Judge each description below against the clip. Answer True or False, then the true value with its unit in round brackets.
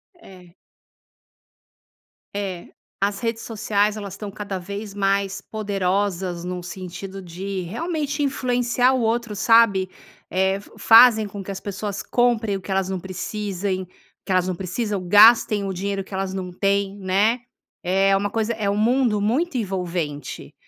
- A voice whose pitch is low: False (200 Hz)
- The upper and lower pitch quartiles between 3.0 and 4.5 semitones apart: False (2.6 semitones)